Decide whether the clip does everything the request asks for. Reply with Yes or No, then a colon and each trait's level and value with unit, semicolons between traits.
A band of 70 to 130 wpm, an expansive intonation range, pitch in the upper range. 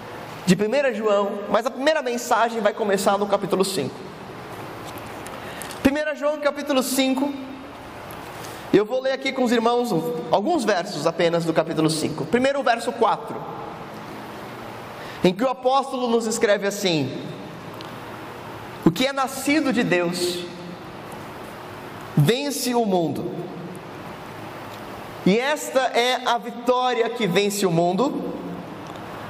Yes: slow, 120 wpm; wide, 6.7 semitones; high, 230 Hz